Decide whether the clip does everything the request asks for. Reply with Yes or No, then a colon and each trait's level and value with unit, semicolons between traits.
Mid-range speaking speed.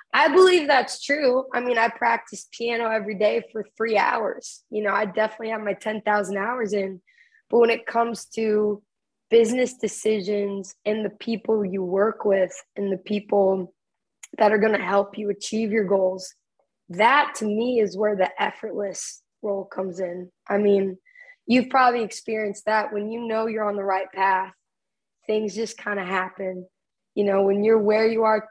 Yes: average, 175 wpm